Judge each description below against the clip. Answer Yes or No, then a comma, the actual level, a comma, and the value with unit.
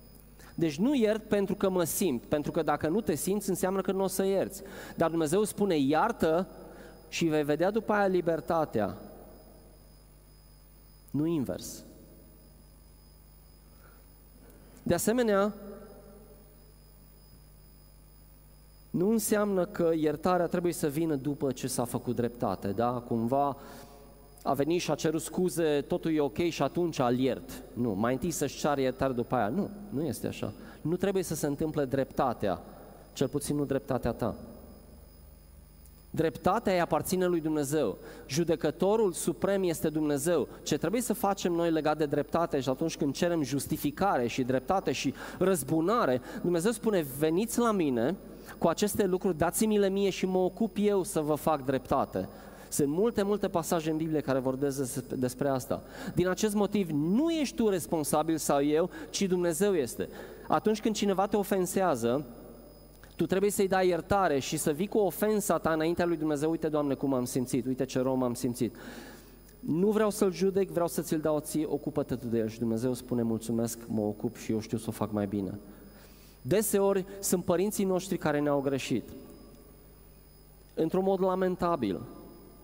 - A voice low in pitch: No, medium, 160 Hz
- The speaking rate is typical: Yes, average, 155 wpm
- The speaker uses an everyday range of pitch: No, wide, 5.9 semitones